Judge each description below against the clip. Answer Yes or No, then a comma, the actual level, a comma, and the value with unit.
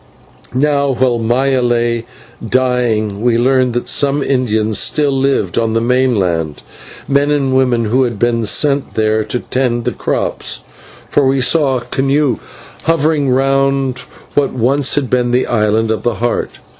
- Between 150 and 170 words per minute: Yes, average, 155 wpm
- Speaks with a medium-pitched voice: No, low, 125 Hz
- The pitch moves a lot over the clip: No, average, 2.8 semitones